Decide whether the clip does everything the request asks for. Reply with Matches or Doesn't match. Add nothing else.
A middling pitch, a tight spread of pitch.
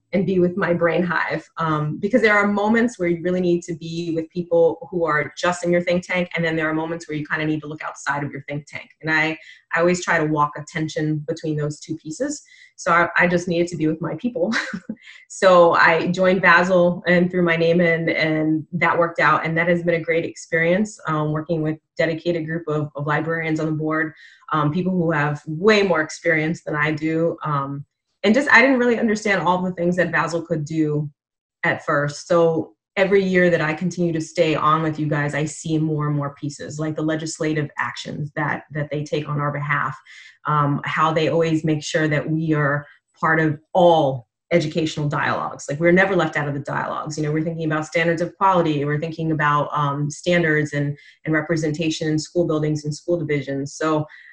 Matches